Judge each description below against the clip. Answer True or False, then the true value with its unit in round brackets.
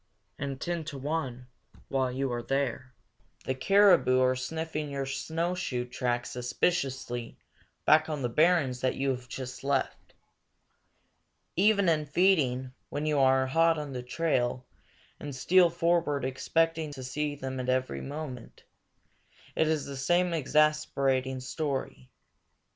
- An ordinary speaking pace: False (130 wpm)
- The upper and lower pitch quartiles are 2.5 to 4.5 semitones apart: True (3.7 semitones)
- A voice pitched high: False (140 Hz)